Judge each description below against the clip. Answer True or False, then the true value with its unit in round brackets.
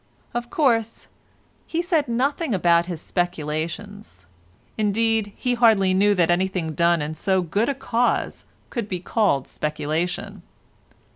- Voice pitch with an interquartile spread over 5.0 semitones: True (5.4 semitones)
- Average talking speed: False (125 wpm)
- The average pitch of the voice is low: False (190 Hz)